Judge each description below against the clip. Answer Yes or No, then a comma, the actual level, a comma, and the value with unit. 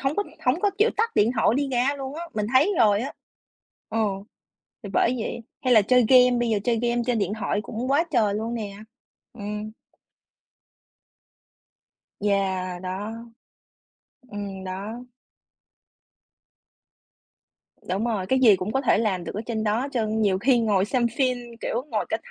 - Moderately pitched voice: No, high, 225 Hz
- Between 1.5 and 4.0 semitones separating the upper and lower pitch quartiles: Yes, average, 3.7 semitones